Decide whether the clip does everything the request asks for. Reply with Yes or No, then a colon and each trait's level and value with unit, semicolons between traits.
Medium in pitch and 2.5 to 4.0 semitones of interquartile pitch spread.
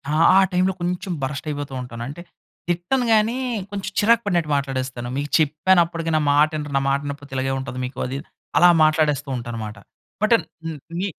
No: medium, 150 Hz; average, 5.0 semitones